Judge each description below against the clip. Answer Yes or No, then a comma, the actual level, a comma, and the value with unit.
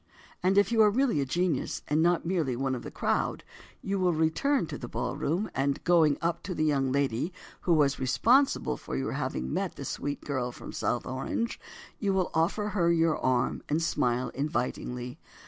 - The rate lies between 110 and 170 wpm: No, average, 190 wpm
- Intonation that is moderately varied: No, wide, 5.8 semitones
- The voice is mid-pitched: Yes, medium, 155 Hz